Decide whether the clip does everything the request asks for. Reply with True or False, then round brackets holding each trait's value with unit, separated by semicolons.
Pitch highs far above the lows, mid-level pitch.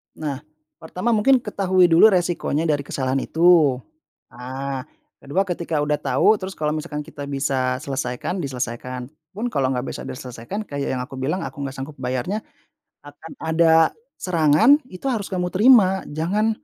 True (5.8 semitones; 155 Hz)